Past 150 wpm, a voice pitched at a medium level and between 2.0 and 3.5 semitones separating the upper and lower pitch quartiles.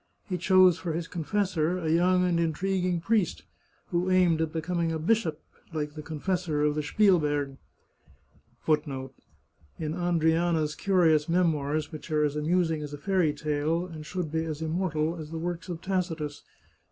Yes: average, 165 wpm; medium, 165 Hz; average, 2.8 semitones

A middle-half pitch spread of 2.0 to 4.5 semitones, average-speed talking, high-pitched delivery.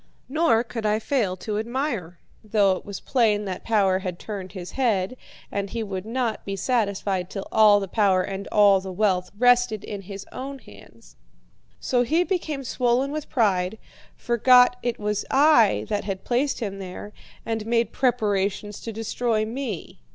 Yes: average, 3.9 semitones; average, 165 wpm; high, 215 Hz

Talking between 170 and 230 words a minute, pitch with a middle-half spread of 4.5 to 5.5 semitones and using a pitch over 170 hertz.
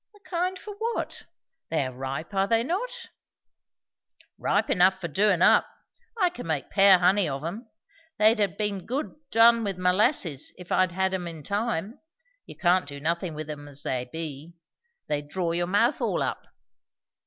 Yes: average, 175 wpm; average, 5.2 semitones; medium, 185 Hz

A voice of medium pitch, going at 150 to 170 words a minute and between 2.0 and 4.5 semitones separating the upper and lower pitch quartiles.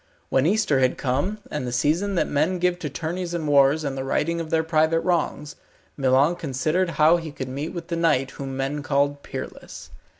No: medium, 150 Hz; average, 200 wpm; average, 3.7 semitones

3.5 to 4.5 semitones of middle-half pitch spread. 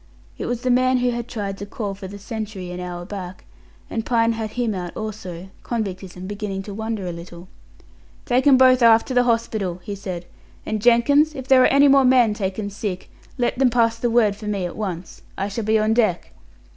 Yes: average, 3.9 semitones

